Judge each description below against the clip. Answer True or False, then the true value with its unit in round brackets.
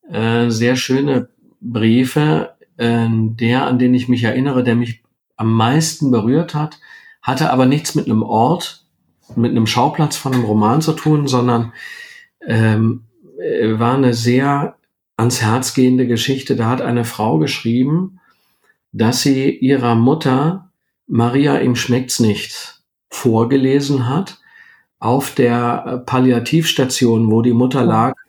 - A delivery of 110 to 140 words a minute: True (125 wpm)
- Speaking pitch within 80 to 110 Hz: False (125 Hz)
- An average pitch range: True (3.1 semitones)